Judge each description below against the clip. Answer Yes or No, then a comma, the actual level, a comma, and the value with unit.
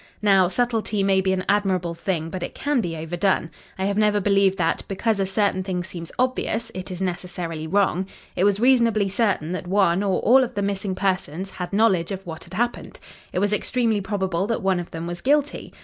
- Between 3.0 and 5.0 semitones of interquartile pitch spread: No, narrow, 2.6 semitones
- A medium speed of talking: No, fast, 210 wpm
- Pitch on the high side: Yes, high, 195 Hz